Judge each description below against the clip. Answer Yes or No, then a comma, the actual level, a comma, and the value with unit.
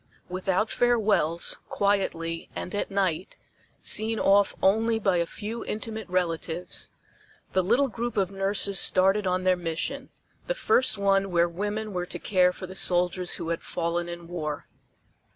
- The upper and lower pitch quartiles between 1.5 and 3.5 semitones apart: Yes, average, 3.1 semitones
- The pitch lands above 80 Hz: Yes, high, 190 Hz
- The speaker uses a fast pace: No, average, 150 wpm